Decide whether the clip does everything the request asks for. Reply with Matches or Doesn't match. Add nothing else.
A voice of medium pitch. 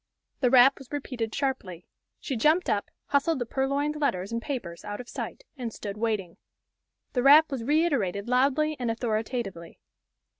Doesn't match